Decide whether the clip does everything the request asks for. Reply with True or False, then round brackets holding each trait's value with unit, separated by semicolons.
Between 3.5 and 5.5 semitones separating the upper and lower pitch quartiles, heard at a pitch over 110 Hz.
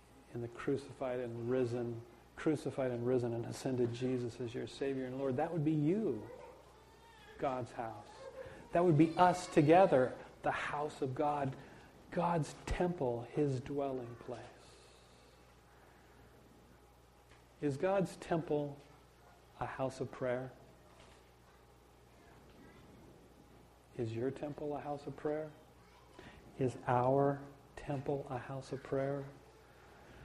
True (3.8 semitones; 135 Hz)